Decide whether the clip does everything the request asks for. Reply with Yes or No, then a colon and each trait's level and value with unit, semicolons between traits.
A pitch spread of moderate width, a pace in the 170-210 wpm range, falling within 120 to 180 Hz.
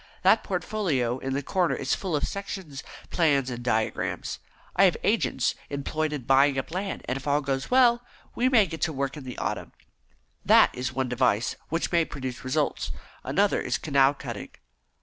Yes: average, 4.3 semitones; average, 180 wpm; medium, 140 Hz